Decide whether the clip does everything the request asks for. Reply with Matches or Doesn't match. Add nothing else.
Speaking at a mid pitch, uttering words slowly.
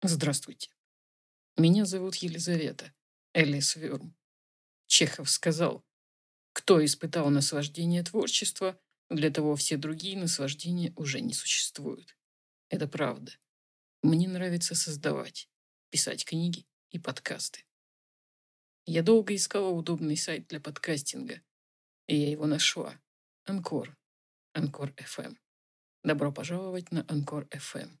Matches